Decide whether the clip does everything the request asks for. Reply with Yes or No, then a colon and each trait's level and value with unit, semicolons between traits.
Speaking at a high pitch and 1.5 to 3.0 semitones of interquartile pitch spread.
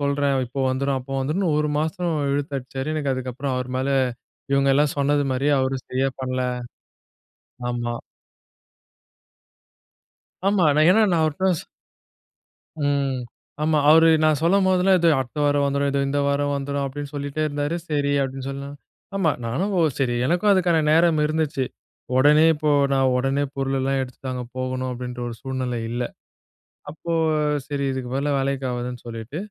No: medium, 140 Hz; average, 2.7 semitones